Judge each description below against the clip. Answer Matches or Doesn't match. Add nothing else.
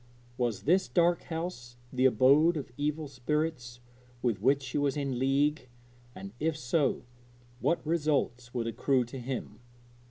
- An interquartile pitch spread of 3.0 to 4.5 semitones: Matches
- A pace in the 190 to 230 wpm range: Doesn't match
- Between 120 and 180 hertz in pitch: Matches